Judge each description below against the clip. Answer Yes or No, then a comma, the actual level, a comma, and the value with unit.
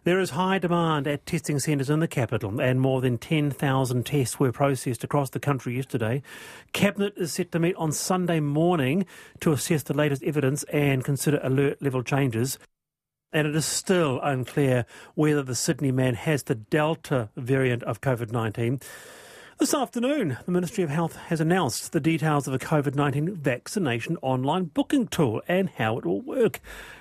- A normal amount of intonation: Yes, average, 4.1 semitones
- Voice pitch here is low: No, medium, 145 Hz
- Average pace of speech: Yes, average, 175 wpm